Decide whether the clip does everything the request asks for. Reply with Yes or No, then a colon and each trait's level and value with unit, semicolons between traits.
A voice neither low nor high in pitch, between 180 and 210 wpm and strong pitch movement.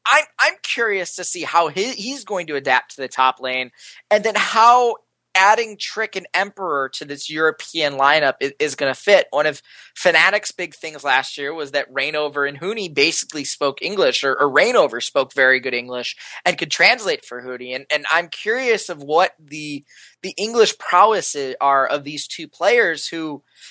Yes: medium, 155 Hz; average, 185 wpm; wide, 6.8 semitones